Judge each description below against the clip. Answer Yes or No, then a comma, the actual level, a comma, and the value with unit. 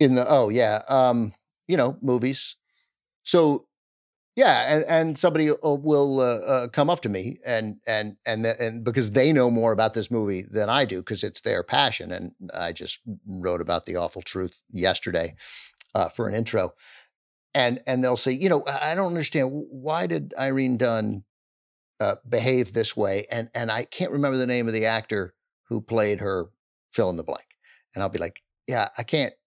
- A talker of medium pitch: No, low, 120 Hz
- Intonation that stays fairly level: No, average, 4.1 semitones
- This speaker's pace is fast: No, average, 190 wpm